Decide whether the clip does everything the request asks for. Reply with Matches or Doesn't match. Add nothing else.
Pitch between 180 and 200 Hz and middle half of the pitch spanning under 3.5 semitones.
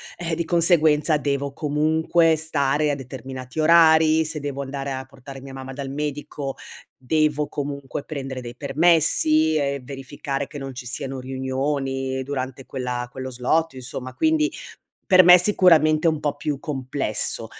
Doesn't match